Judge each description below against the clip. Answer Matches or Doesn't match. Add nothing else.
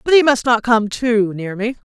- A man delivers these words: Doesn't match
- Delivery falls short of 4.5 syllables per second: Doesn't match